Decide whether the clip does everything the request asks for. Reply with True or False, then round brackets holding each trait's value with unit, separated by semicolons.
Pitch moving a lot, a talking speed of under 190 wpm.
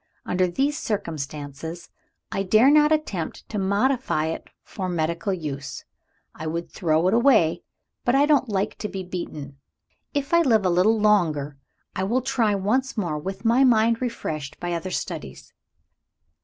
True (6.3 semitones; 155 wpm)